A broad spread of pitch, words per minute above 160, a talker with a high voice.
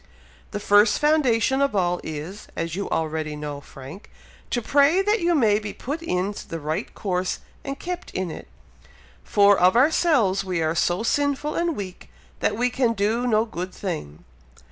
Yes: wide, 7.5 semitones; average, 170 wpm; high, 205 Hz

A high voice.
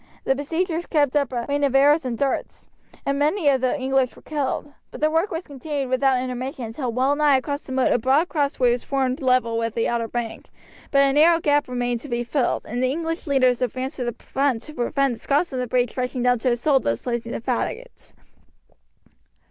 Yes: very high, 265 Hz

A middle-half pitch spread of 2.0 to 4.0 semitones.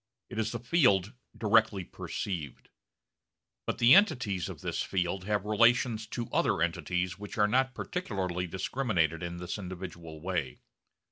No: average, 4.4 semitones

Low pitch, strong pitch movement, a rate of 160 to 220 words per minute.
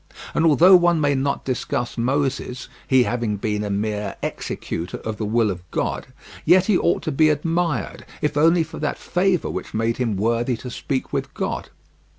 Yes: low, 130 Hz; wide, 5.9 semitones; average, 180 wpm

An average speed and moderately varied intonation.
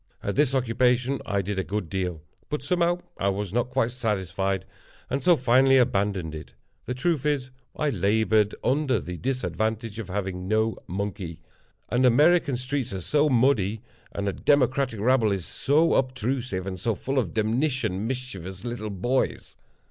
Yes: average, 155 wpm; average, 4.9 semitones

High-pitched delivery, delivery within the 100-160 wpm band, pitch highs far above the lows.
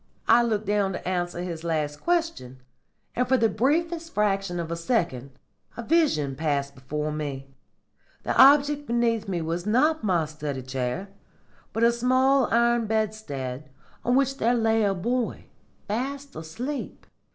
Yes: high, 210 Hz; average, 150 wpm; wide, 8.2 semitones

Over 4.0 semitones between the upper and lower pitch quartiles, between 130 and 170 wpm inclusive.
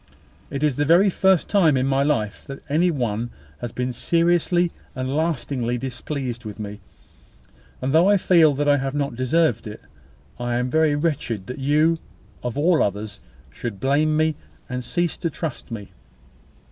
Yes: average, 4.6 semitones; average, 165 wpm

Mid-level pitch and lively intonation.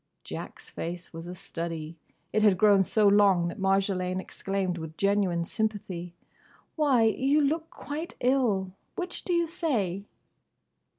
No: high, 195 Hz; wide, 5.8 semitones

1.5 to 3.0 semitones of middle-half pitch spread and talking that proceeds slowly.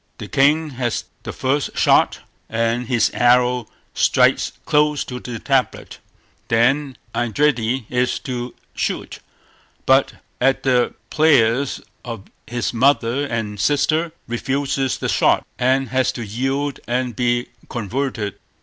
Yes: narrow, 2.5 semitones; slow, 120 wpm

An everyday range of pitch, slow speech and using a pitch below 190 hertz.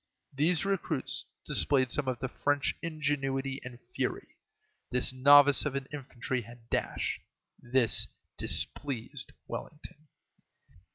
No: narrow, 2.2 semitones; slow, 110 wpm; low, 135 Hz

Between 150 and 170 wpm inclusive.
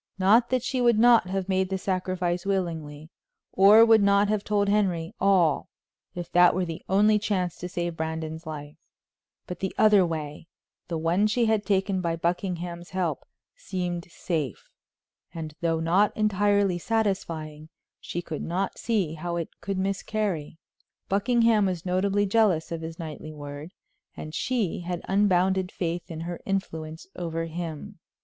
Yes: average, 155 wpm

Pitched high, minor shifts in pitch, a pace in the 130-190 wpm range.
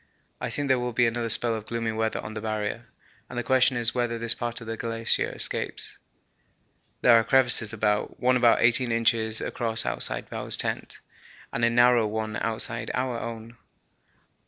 No: low, 115 Hz; narrow, 1.4 semitones; average, 180 wpm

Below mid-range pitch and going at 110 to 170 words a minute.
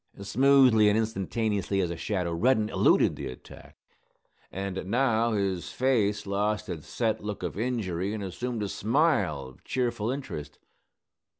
Yes: low, 105 Hz; average, 140 wpm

